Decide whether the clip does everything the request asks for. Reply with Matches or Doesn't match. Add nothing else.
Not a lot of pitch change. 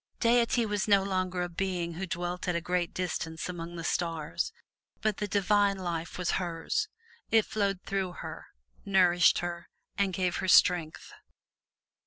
Matches